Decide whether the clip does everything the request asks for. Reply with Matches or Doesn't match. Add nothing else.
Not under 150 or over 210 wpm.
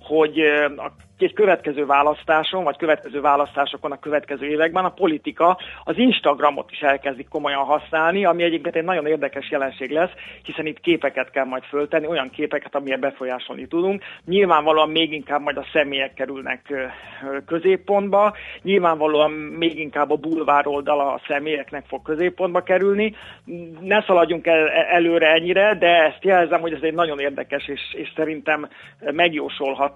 Doesn't match